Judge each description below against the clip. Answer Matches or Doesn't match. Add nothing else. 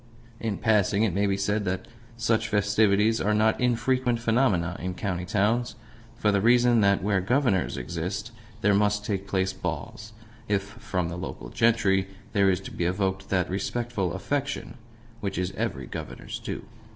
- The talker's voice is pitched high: Doesn't match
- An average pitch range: Matches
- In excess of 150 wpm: Matches